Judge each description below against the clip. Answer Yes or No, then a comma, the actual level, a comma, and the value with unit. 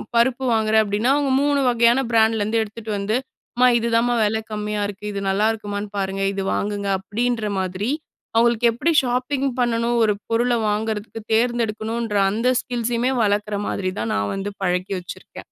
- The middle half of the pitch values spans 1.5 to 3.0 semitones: Yes, narrow, 2.5 semitones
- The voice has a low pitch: No, high, 220 Hz